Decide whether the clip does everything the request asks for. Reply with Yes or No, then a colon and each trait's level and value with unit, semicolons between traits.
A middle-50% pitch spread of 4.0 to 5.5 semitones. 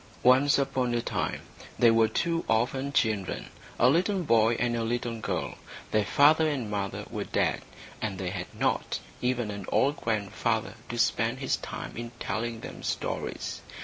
No: average, 3.1 semitones